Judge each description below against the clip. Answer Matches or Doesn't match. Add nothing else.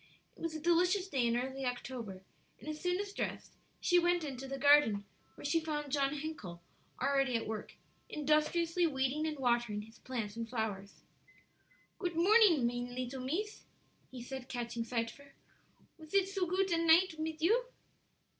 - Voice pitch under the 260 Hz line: Doesn't match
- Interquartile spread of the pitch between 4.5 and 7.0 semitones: Matches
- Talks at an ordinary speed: Matches